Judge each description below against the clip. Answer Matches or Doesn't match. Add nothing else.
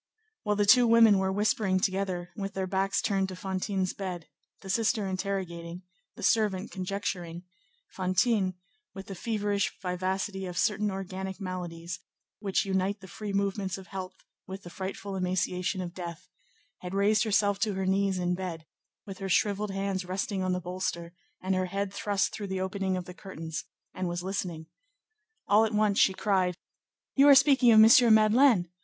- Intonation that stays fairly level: Matches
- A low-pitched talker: Doesn't match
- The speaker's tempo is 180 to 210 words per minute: Doesn't match